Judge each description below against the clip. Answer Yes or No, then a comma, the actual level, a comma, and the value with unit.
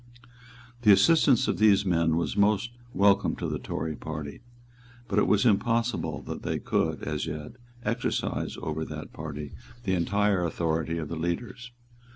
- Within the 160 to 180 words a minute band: No, average, 150 wpm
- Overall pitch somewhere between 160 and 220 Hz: No, very low, 90 Hz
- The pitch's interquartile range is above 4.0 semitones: Yes, average, 4.9 semitones